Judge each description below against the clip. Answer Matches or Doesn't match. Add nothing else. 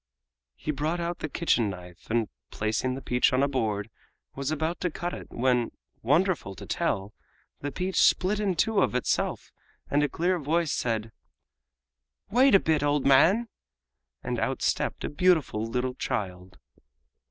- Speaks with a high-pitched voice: Doesn't match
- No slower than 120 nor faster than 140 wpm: Doesn't match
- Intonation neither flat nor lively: Doesn't match